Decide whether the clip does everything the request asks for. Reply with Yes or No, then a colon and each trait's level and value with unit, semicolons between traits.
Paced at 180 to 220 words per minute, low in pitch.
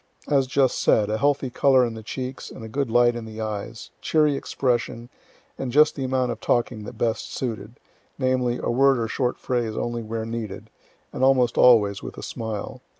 Yes: average, 190 wpm; low, 120 Hz